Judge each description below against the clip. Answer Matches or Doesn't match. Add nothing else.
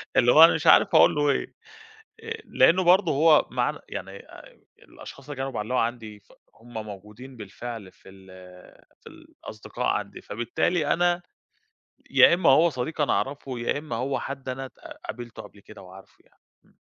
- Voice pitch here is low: Matches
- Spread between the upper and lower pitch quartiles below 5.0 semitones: Doesn't match